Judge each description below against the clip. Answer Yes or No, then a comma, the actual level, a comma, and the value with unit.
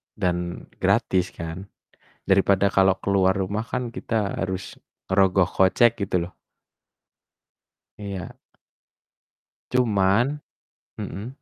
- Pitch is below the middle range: Yes, very low, 95 Hz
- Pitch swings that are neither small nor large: No, narrow, 1.8 semitones